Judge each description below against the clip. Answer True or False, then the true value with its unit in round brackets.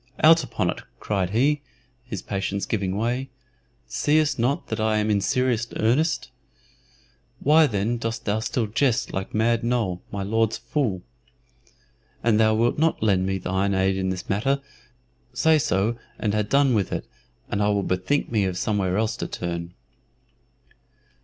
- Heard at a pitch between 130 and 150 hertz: False (110 Hz)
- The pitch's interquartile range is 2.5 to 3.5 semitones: False (4.0 semitones)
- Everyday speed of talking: True (160 wpm)